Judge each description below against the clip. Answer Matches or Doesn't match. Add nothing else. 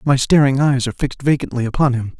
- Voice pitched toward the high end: Doesn't match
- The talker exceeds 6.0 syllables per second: Matches